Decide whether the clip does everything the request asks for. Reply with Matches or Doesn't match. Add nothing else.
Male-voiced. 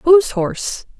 Doesn't match